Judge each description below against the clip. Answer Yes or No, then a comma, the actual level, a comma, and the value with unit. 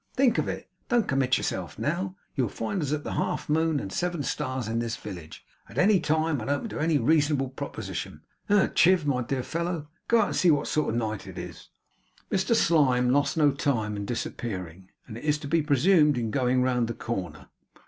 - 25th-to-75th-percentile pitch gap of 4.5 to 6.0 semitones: Yes, wide, 5.5 semitones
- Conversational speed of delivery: No, fast, 210 wpm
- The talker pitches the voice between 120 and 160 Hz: Yes, medium, 140 Hz